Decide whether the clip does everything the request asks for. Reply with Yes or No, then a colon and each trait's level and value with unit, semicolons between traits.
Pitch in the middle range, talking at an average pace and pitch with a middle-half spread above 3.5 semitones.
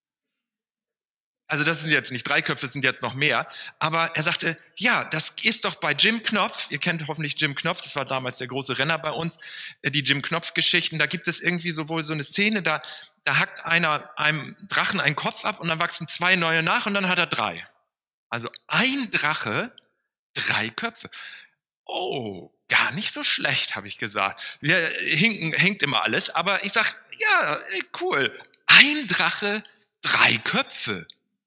Yes: medium, 165 Hz; average, 180 wpm; average, 5.3 semitones